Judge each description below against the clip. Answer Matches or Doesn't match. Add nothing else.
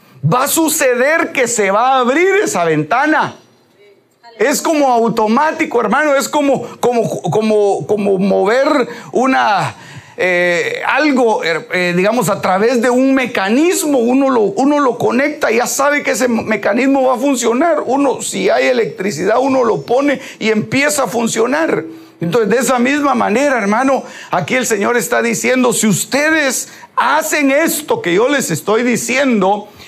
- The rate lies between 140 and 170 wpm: Matches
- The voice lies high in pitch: Matches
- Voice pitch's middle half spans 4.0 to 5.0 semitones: Matches